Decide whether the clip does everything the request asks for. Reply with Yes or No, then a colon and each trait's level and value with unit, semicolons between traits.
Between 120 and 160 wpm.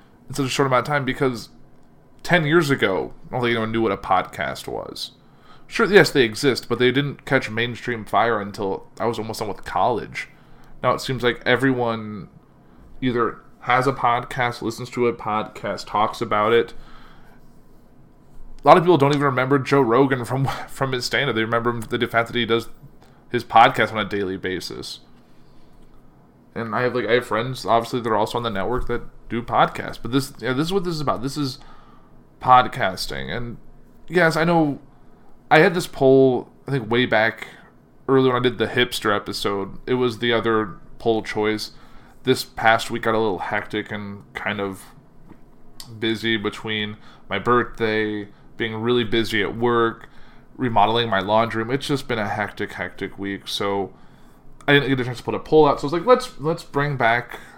No: average, 190 wpm